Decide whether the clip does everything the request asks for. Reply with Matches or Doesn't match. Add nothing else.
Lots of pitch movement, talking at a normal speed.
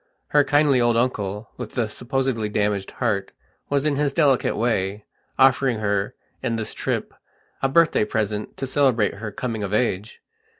Doesn't match